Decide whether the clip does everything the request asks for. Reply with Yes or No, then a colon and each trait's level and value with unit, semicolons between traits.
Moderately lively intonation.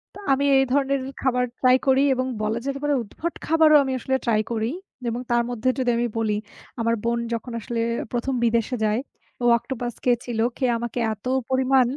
No: narrow, 2.3 semitones